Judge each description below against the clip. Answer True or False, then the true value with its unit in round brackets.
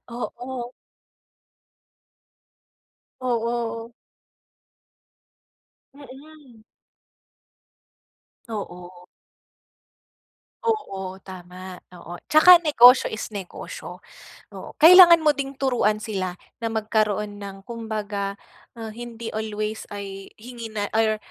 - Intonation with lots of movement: False (3.6 semitones)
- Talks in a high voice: True (225 Hz)